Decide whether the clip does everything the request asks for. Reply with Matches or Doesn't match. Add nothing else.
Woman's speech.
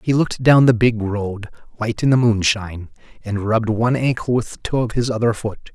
Doesn't match